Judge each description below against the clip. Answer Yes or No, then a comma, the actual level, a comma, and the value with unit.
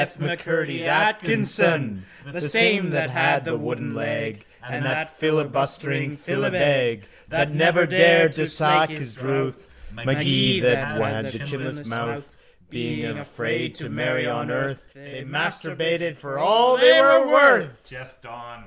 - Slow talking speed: Yes, slow, 130 wpm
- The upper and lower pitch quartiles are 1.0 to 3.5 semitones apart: No, average, 4.1 semitones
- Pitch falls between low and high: Yes, medium, 145 Hz